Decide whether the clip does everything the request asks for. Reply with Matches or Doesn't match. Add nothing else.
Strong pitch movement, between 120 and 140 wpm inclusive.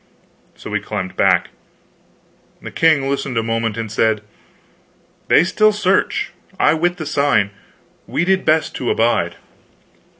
Matches